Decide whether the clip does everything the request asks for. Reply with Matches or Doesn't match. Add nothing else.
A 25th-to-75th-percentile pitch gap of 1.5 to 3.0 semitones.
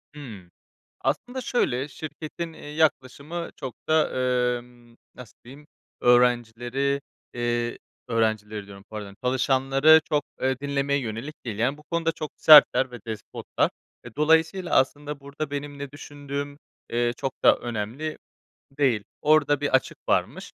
Doesn't match